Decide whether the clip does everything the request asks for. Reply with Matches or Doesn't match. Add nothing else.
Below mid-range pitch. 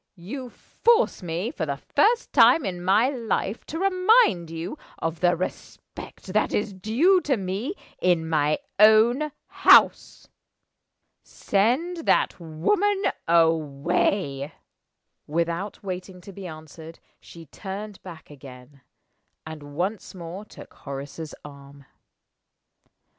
Doesn't match